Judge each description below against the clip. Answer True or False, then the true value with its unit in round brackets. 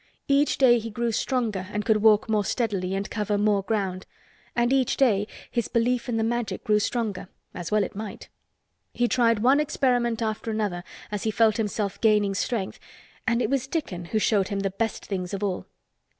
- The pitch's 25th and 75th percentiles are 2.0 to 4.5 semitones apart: True (2.8 semitones)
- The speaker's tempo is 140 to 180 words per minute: False (190 wpm)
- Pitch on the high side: True (215 Hz)